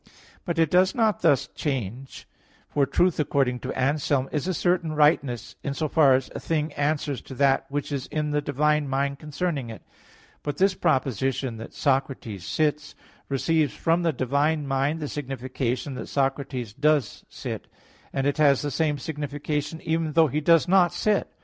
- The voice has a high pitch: No, medium, 145 Hz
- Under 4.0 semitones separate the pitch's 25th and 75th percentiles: Yes, narrow, 2.6 semitones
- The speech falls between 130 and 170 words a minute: No, average, 180 wpm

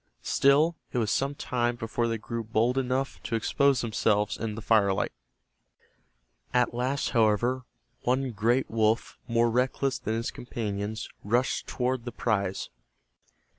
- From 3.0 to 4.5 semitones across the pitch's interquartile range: No, narrow, 2.6 semitones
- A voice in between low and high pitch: No, low, 120 Hz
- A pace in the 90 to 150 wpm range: Yes, slow, 135 wpm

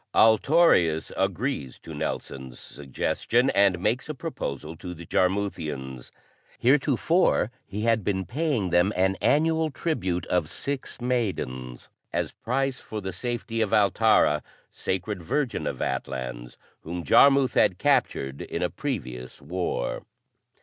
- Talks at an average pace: No, slow, 125 wpm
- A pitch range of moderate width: No, wide, 7.9 semitones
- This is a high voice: No, very low, 95 Hz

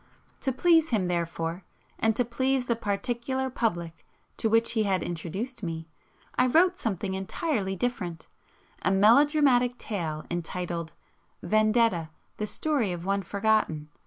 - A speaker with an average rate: No, slow, 130 wpm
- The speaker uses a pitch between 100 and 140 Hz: No, high, 215 Hz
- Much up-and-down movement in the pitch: Yes, wide, 5.8 semitones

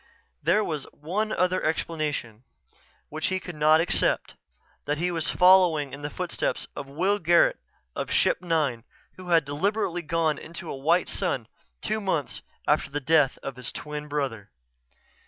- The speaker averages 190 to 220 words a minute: No, average, 155 wpm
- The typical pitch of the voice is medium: Yes, medium, 160 Hz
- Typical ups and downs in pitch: Yes, average, 3.6 semitones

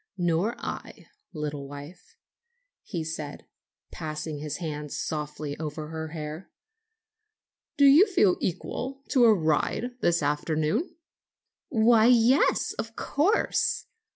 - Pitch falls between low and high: Yes, medium, 165 Hz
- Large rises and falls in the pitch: Yes, wide, 7.6 semitones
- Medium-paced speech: No, slow, 110 wpm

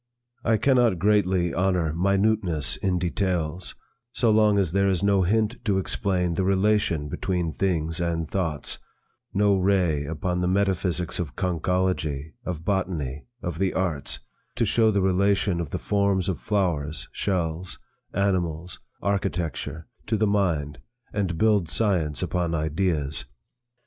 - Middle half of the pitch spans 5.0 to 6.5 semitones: No, average, 3.3 semitones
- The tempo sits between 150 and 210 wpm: No, slow, 135 wpm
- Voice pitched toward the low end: Yes, very low, 90 Hz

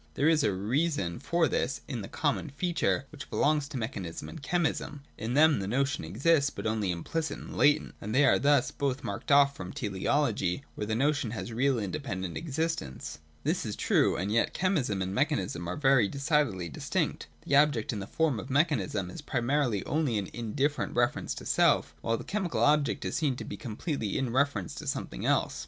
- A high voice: No, low, 135 Hz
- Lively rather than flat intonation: Yes, wide, 6.0 semitones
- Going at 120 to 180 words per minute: No, average, 195 wpm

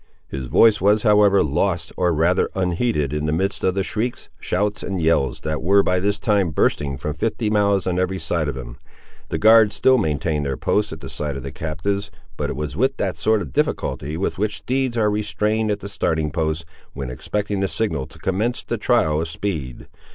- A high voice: No, very low, 95 Hz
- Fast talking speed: Yes, fast, 210 wpm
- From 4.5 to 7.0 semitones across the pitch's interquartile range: Yes, average, 5.3 semitones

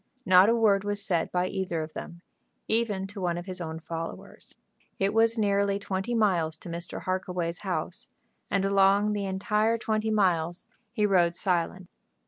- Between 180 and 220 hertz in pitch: Yes, high, 190 Hz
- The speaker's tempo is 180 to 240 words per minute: No, average, 165 wpm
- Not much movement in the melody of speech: No, average, 3.0 semitones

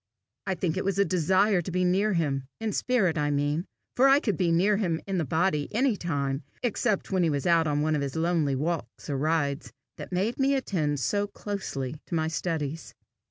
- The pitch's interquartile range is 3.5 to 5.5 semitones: Yes, average, 4.9 semitones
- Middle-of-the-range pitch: Yes, medium, 170 Hz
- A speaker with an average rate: No, fast, 210 wpm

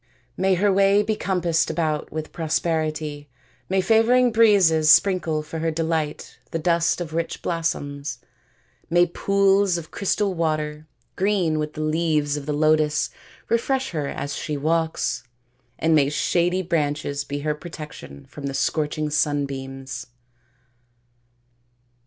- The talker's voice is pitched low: No, medium, 160 Hz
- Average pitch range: Yes, average, 3.2 semitones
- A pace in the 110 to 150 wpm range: Yes, slow, 135 wpm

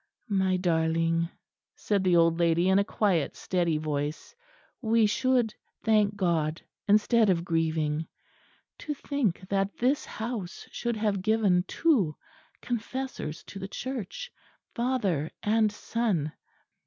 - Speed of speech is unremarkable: No, slow, 120 wpm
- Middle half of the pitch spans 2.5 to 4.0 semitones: No, average, 5.1 semitones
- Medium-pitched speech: No, high, 195 Hz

